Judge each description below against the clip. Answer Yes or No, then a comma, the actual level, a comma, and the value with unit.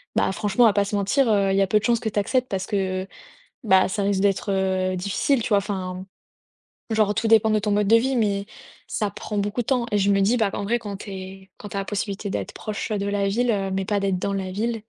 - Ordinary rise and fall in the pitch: No, narrow, 1.9 semitones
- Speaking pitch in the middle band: No, high, 200 Hz